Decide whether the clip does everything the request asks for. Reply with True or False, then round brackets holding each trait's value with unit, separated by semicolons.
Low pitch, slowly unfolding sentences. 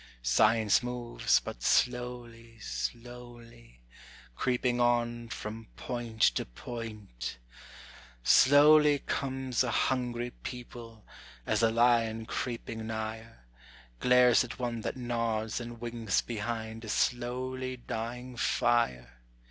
True (120 Hz; 100 wpm)